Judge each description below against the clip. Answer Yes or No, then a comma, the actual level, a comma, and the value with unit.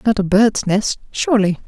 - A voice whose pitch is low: No, high, 210 Hz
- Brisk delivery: No, average, 180 wpm